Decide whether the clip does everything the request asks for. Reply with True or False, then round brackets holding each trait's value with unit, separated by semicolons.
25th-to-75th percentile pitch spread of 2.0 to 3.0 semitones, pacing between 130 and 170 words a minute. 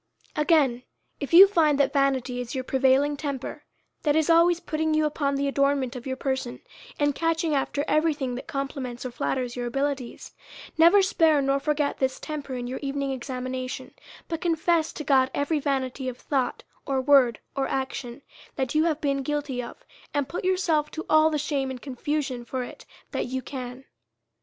False (2.7 semitones; 180 wpm)